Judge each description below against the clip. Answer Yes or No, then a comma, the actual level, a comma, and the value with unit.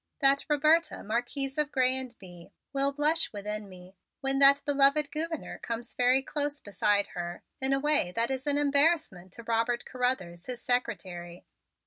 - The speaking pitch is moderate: No, very high, 260 Hz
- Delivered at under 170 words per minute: Yes, average, 160 wpm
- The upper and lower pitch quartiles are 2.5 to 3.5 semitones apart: No, average, 5.2 semitones